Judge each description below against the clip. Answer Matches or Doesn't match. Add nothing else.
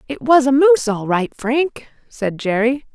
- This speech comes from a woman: Matches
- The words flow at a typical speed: Matches